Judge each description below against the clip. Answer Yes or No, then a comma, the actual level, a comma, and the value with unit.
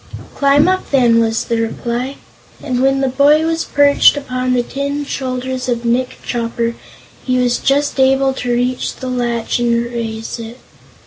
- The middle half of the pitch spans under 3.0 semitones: Yes, narrow, 2.5 semitones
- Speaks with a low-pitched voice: No, very high, 255 Hz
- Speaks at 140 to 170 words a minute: Yes, average, 165 wpm